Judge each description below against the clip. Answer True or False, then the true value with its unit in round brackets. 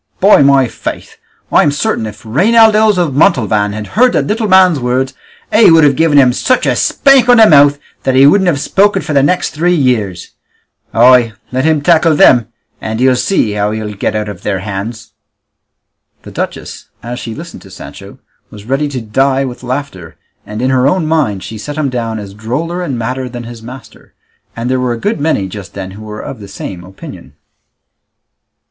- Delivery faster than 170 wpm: True (195 wpm)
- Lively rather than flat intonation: True (6.4 semitones)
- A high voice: False (130 Hz)